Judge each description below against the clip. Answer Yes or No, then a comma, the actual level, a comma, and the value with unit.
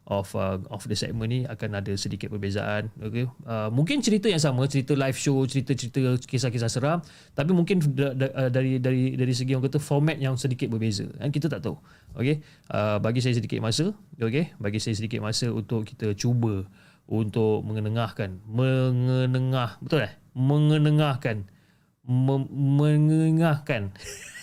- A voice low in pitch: Yes, low, 130 Hz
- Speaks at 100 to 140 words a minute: No, average, 150 wpm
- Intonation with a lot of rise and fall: No, average, 4.4 semitones